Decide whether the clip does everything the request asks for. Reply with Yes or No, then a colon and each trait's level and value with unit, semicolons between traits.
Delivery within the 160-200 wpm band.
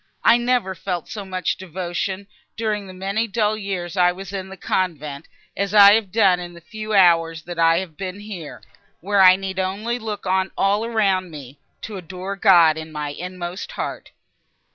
Yes: average, 180 wpm